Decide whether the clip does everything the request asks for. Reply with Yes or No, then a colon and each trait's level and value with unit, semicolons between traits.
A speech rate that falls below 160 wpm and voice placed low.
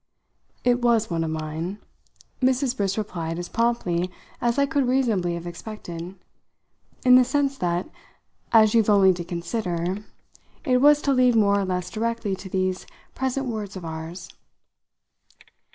No: average, 150 wpm; high, 205 Hz